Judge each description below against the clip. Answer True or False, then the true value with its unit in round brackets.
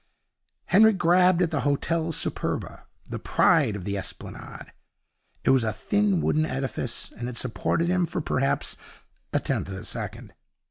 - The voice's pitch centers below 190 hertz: True (140 Hz)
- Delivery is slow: False (155 wpm)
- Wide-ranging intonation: True (7.5 semitones)